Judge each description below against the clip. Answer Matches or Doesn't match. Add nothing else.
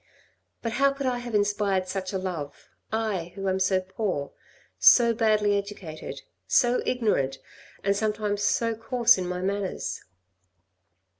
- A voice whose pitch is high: Matches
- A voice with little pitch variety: Doesn't match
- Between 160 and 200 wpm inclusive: Doesn't match